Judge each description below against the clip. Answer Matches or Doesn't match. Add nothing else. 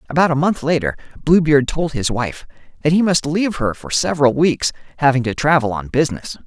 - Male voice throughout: Matches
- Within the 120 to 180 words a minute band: Doesn't match